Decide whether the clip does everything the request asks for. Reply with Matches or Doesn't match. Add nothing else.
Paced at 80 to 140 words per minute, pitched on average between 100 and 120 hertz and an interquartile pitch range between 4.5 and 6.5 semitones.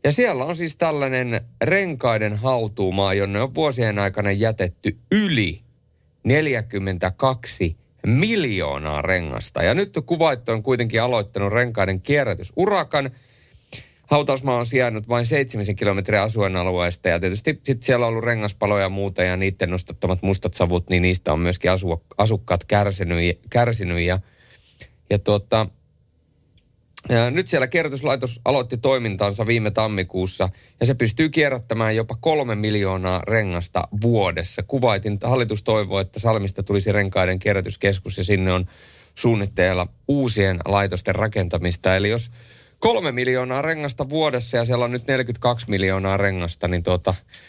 Matches